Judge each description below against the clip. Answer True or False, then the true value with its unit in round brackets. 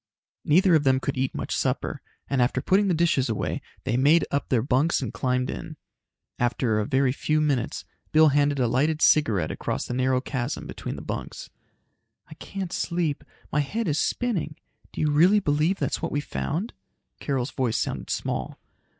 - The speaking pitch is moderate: True (145 Hz)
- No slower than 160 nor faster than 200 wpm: True (180 wpm)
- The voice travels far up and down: False (3.7 semitones)